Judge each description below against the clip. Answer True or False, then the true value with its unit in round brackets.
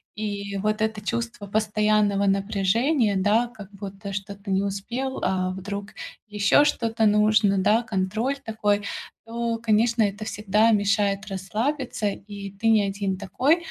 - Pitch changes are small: True (2.1 semitones)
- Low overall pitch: False (210 Hz)